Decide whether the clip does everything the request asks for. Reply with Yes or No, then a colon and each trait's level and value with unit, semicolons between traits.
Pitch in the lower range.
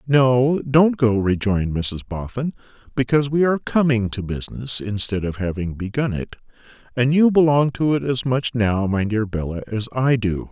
Yes: low, 120 Hz